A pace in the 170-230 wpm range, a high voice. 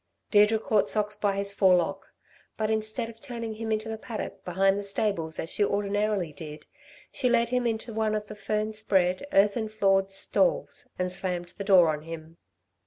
Yes: average, 180 wpm; high, 205 Hz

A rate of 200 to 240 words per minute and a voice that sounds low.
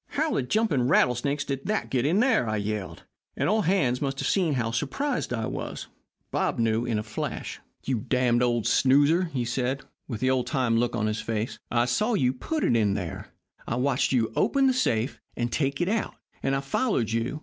Yes: fast, 205 wpm; low, 125 Hz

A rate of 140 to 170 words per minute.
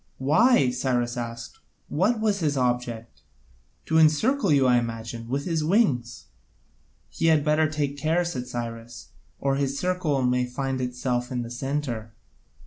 Yes: average, 145 wpm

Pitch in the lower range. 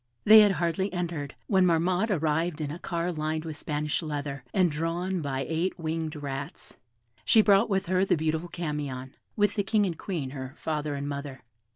No: medium, 160 Hz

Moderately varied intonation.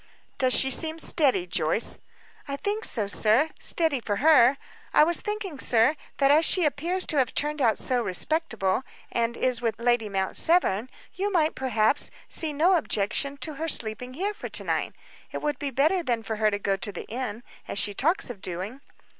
No: wide, 6.3 semitones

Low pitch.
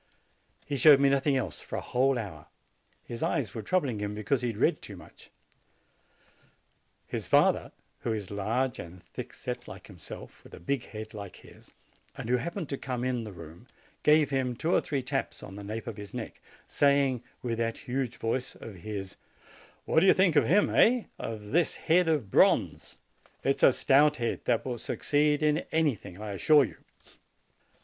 Yes: low, 125 Hz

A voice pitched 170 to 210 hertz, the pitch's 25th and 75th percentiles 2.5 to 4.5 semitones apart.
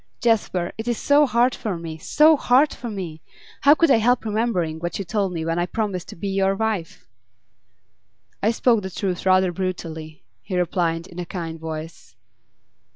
No: high, 190 Hz; average, 5.1 semitones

